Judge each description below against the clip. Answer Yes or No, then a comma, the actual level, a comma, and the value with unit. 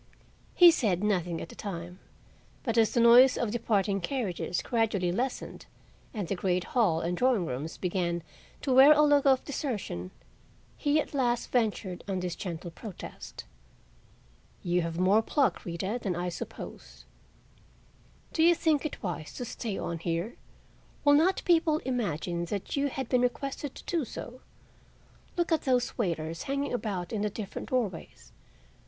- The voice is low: No, high, 215 Hz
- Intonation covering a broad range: Yes, wide, 6.8 semitones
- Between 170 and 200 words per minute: No, average, 160 wpm